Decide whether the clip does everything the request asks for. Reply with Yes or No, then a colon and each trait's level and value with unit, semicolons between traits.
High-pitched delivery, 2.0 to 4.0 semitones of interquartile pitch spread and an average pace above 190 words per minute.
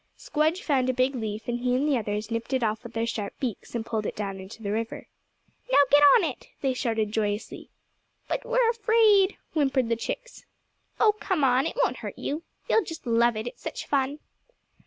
No: very high, 250 Hz; average, 5.0 semitones; fast, 205 wpm